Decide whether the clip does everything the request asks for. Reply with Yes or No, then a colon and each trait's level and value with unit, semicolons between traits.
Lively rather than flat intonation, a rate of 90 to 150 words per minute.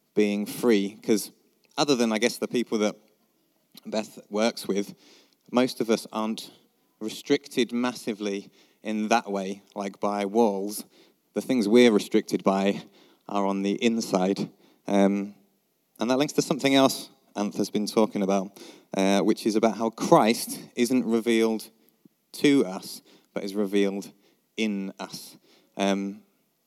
No: average, 2.8 semitones; slow, 135 wpm